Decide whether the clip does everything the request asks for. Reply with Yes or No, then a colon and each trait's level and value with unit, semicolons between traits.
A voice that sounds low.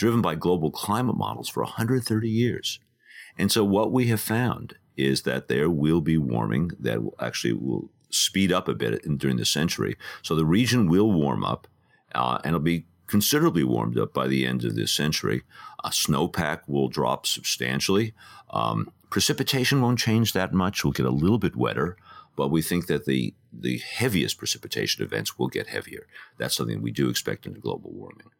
Yes: very low, 90 Hz